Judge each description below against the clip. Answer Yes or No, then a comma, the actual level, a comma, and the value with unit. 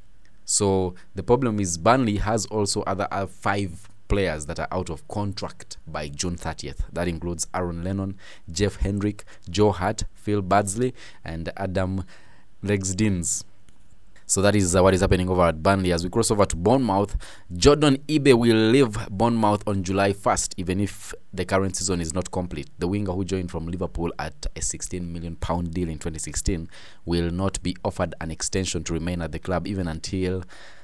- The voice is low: Yes, very low, 95 Hz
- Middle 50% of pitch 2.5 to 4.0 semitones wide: Yes, average, 2.8 semitones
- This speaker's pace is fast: No, average, 175 wpm